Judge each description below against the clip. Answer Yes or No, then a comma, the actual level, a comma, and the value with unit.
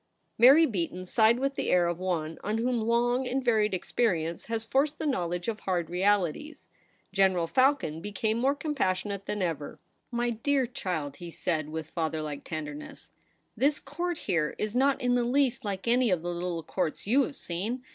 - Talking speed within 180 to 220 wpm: Yes, average, 185 wpm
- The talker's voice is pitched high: Yes, high, 210 Hz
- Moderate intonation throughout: No, wide, 6.4 semitones